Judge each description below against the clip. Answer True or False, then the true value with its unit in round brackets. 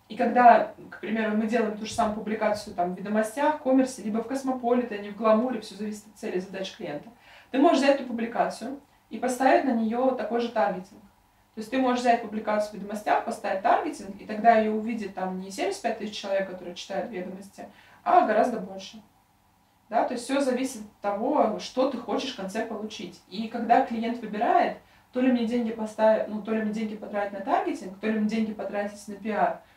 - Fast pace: True (205 wpm)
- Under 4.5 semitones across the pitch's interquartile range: True (3.0 semitones)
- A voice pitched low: False (220 Hz)